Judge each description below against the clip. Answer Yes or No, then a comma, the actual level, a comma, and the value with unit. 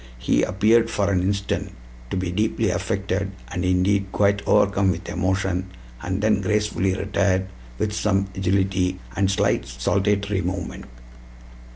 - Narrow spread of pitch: Yes, narrow, 1.5 semitones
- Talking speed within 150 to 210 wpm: No, average, 140 wpm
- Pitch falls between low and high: No, very low, 95 Hz